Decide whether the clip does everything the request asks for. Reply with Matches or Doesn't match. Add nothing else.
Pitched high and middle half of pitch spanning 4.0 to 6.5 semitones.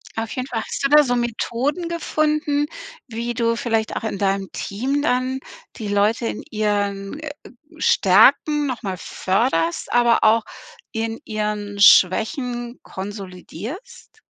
Matches